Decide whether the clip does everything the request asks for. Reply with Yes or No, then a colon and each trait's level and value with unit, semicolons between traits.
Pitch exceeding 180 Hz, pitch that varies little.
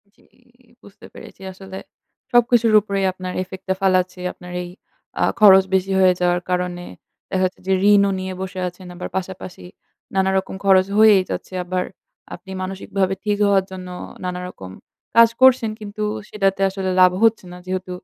Yes: high, 190 Hz; narrow, 1.5 semitones